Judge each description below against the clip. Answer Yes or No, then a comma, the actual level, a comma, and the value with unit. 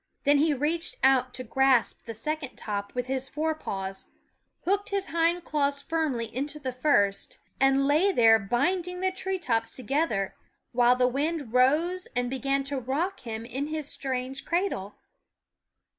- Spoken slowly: No, average, 160 wpm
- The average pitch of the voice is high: Yes, very high, 270 Hz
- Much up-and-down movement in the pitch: No, average, 4.3 semitones